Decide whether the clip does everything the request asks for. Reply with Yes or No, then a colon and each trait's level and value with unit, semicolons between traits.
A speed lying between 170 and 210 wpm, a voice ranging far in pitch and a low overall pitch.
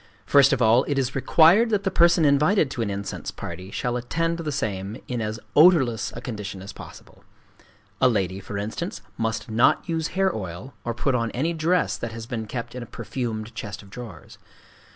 Yes: average, 195 wpm; wide, 5.9 semitones; low, 120 Hz